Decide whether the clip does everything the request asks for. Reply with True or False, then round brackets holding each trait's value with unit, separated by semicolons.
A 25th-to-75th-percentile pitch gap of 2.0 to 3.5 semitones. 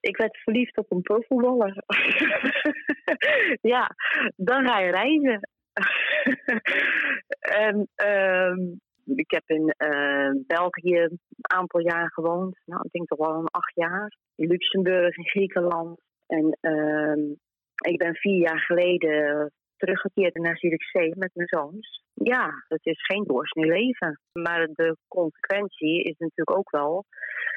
False (4.8 semitones)